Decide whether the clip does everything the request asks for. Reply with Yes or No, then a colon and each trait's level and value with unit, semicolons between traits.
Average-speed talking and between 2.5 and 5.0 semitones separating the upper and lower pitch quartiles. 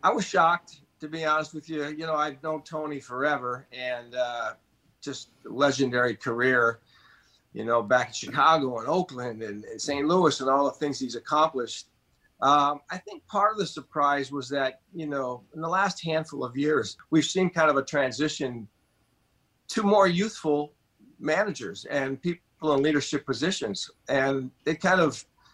Yes: average, 170 wpm; average, 3.4 semitones